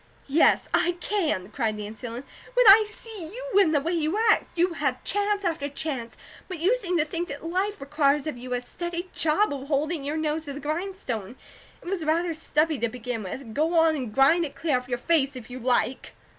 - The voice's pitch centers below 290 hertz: No, very high, 310 Hz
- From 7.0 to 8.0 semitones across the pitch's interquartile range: No, average, 5.2 semitones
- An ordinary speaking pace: No, fast, 215 wpm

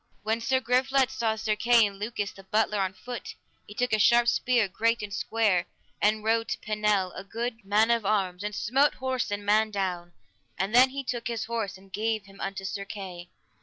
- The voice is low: No, high, 215 Hz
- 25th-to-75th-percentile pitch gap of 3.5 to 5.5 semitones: No, average, 3.0 semitones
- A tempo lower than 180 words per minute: No, fast, 205 wpm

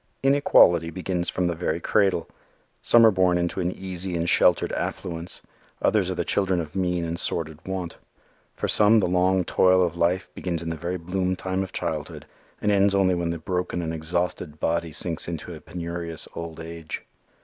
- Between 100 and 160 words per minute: No, average, 185 wpm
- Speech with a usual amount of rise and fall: No, narrow, 1.9 semitones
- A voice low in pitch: Yes, very low, 90 Hz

